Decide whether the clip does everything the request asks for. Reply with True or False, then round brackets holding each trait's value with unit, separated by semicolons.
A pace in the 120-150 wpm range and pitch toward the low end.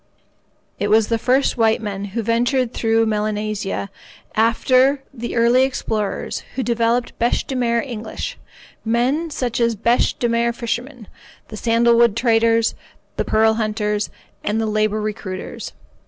False (140 wpm; 230 Hz)